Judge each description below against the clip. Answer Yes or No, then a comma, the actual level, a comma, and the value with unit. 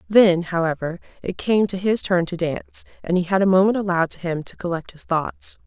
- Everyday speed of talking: No, fast, 225 wpm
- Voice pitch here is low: No, medium, 180 Hz